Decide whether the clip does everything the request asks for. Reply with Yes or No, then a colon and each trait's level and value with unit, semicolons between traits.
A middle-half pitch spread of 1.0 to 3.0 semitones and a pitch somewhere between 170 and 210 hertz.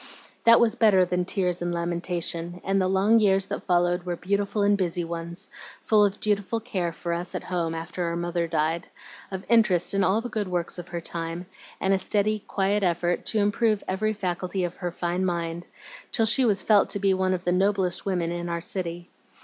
Yes: average, 2.7 semitones; medium, 185 Hz